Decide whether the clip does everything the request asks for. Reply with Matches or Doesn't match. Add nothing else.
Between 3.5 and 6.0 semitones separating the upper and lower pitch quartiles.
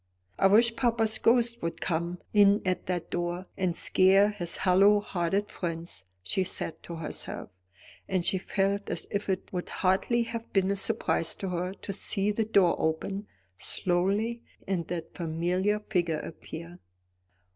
Doesn't match